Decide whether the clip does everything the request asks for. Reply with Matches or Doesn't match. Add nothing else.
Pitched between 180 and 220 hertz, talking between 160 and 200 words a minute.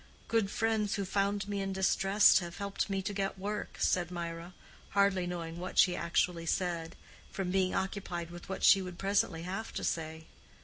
Matches